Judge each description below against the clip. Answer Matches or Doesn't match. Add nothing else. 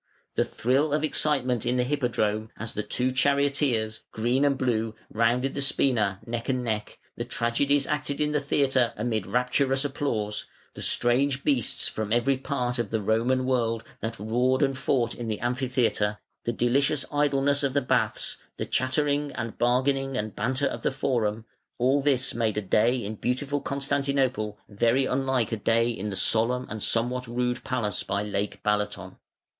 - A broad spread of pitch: Doesn't match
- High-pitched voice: Doesn't match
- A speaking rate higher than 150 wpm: Matches